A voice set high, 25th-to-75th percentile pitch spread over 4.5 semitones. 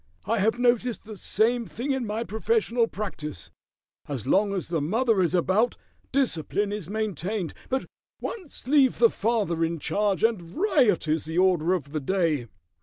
Yes: high, 205 Hz; wide, 5.6 semitones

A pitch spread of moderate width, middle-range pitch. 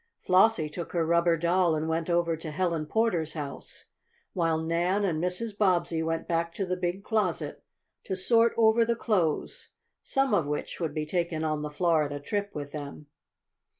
Yes: average, 3.0 semitones; medium, 170 Hz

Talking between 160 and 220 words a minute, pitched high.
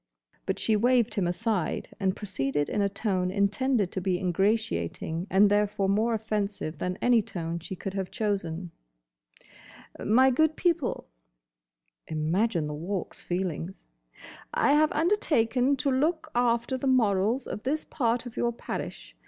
No: slow, 135 wpm; high, 205 Hz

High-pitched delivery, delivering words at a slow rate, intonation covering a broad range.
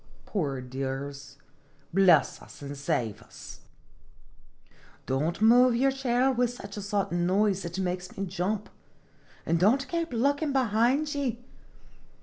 Yes: high, 200 Hz; slow, 130 wpm; wide, 6.5 semitones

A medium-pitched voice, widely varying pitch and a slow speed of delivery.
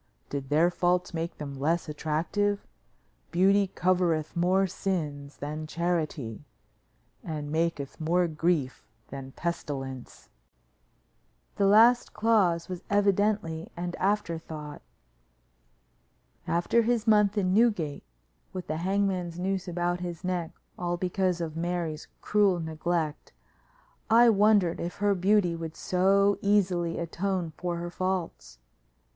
No: medium, 175 Hz; average, 3.3 semitones; slow, 115 wpm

